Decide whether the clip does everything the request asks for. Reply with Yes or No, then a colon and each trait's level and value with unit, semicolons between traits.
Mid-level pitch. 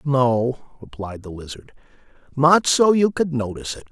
No: low, 130 Hz